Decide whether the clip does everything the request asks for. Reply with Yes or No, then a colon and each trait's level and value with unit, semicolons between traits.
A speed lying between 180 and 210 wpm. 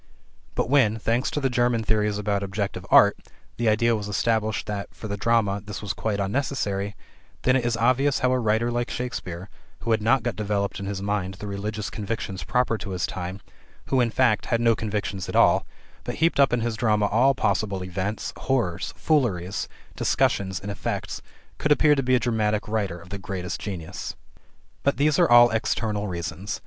Yes: average, 190 wpm